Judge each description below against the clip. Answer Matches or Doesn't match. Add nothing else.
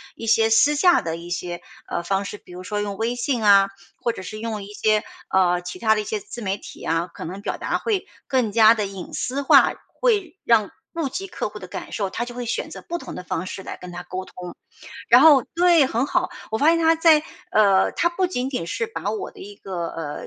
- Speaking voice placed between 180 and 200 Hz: Doesn't match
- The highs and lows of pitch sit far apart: Matches